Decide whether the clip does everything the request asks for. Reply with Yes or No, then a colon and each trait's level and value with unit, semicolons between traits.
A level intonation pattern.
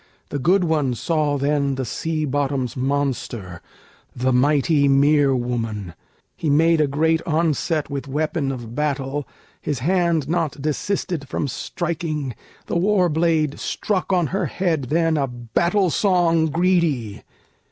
No: average, 3.6 semitones